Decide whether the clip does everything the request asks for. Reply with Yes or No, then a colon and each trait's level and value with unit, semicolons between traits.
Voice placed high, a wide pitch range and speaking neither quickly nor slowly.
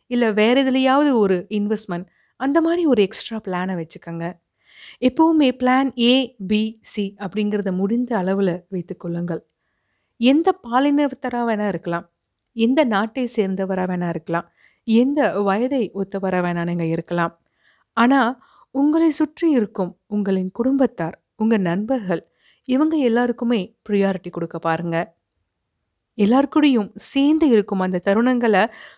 Yes: high, 210 Hz; wide, 5.9 semitones; average, 110 wpm